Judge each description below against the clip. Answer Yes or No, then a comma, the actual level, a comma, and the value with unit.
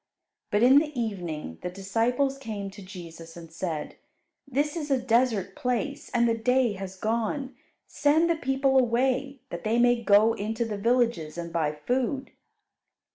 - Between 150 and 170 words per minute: Yes, average, 160 wpm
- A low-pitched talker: No, high, 230 Hz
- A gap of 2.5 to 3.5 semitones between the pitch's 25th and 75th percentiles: No, average, 5.3 semitones